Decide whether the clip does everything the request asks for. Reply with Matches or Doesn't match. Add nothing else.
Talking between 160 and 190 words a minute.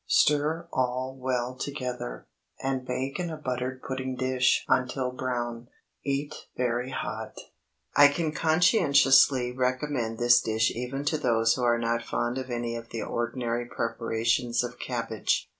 Doesn't match